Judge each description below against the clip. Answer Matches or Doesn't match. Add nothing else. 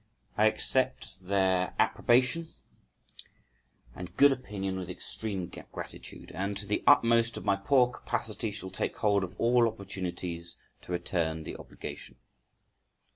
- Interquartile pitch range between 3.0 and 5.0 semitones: Matches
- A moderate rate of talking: Doesn't match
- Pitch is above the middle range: Doesn't match